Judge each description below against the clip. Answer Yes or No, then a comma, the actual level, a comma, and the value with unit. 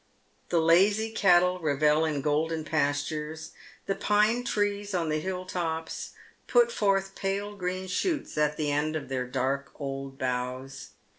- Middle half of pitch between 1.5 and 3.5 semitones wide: No, average, 5.0 semitones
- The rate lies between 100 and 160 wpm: Yes, average, 145 wpm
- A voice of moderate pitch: Yes, medium, 160 Hz